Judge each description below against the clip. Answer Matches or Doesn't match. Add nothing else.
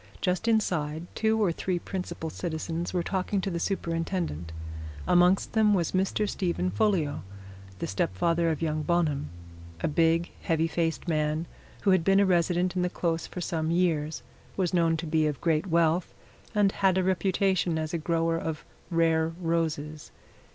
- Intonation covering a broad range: Doesn't match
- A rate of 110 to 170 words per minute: Matches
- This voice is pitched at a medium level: Matches